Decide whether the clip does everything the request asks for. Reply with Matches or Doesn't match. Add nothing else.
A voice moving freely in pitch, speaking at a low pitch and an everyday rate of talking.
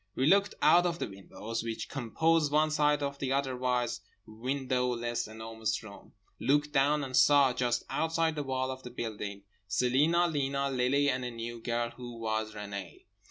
Doesn't match